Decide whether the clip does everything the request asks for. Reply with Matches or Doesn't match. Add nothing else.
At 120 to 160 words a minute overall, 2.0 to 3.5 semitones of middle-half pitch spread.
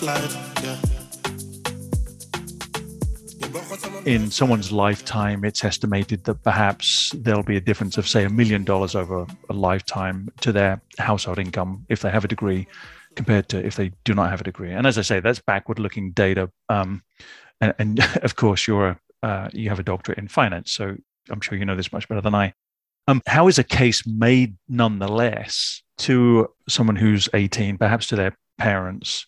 Doesn't match